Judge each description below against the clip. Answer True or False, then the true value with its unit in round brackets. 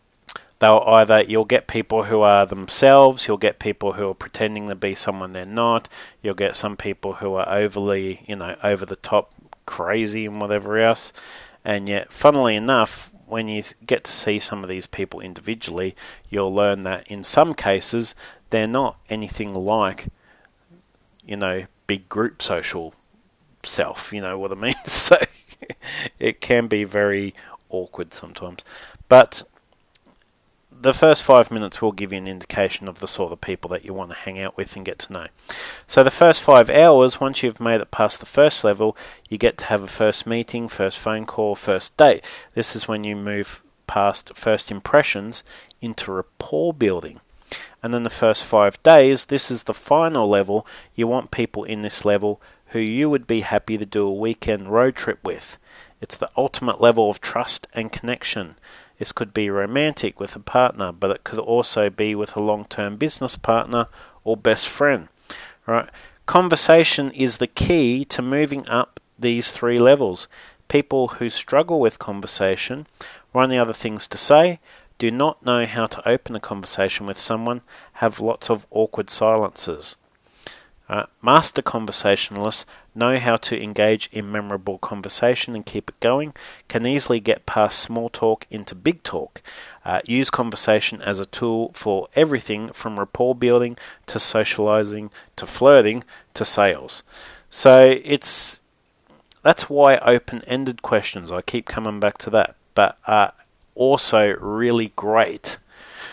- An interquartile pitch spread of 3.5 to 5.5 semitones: False (3.0 semitones)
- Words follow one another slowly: False (165 wpm)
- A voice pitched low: True (110 Hz)